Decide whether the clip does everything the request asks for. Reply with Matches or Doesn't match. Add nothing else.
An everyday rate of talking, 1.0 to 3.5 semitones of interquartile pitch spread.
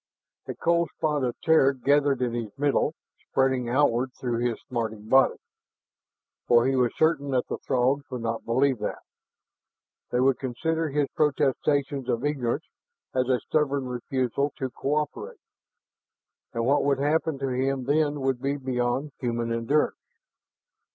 Matches